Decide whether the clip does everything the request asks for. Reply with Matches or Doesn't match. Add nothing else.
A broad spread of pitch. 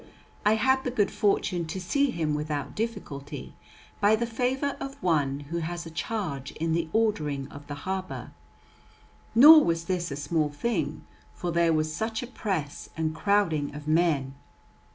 Matches